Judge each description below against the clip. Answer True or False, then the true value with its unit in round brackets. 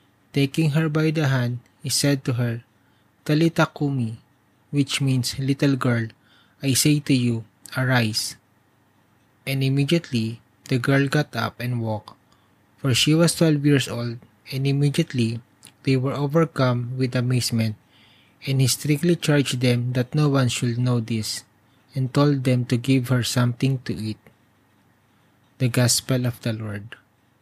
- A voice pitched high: False (125 Hz)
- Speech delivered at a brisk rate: False (140 wpm)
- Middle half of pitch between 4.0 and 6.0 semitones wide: False (3.2 semitones)